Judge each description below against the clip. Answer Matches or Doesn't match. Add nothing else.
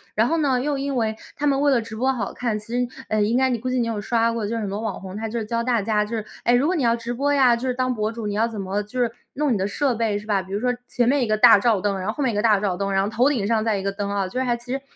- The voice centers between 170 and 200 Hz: Doesn't match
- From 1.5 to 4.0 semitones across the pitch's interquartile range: Matches